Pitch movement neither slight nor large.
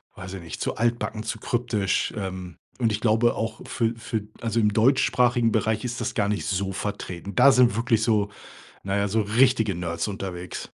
Yes: average, 3.0 semitones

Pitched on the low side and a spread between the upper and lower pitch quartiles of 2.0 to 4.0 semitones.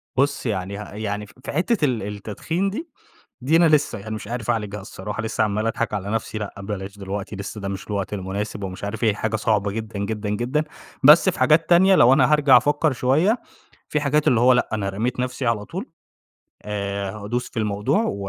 No: low, 110 Hz; average, 4.8 semitones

